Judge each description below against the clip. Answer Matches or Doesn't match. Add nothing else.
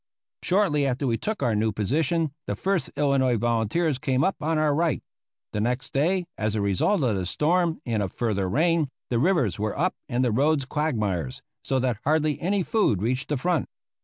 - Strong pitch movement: Matches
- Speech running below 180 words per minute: Doesn't match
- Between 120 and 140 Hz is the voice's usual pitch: Matches